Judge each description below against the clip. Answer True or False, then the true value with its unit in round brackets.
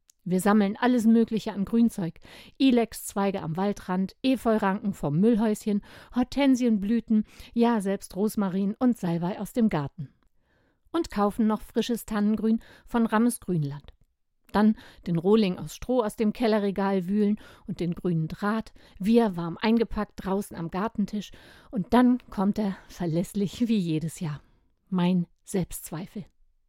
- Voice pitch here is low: False (205 Hz)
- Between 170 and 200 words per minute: False (130 wpm)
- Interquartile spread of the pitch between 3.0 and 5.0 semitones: True (3.4 semitones)